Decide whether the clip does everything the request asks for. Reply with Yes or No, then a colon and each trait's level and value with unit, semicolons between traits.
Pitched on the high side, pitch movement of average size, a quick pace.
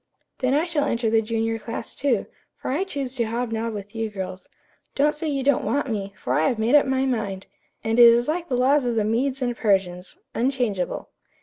Yes: high, 235 Hz; average, 3.7 semitones; fast, 220 wpm